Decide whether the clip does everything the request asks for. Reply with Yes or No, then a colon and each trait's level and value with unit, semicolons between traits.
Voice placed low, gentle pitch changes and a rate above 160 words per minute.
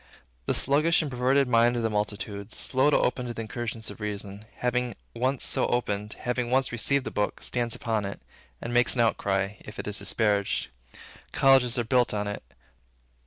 No: low, 120 Hz; average, 3.0 semitones; average, 185 wpm